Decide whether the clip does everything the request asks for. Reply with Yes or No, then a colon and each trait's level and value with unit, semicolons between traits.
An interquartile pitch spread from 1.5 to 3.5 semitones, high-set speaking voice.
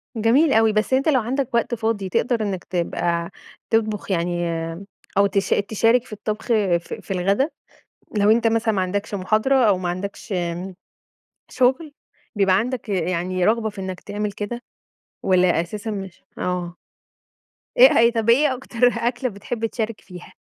No: average, 3.9 semitones; high, 210 Hz